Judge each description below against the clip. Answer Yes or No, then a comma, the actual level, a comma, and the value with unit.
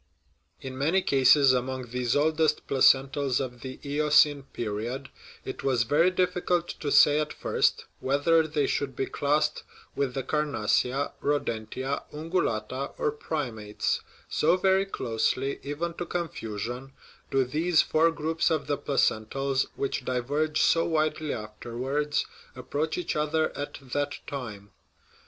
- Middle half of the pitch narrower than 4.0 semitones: Yes, average, 3.3 semitones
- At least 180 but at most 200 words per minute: No, slow, 135 wpm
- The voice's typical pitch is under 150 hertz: Yes, medium, 140 Hz